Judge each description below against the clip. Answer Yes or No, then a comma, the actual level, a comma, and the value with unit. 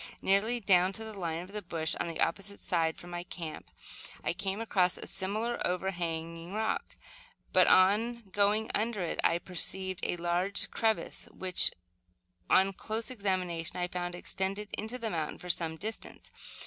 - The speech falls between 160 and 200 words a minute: Yes, average, 165 wpm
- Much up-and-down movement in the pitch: No, average, 3.2 semitones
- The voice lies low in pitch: No, high, 190 Hz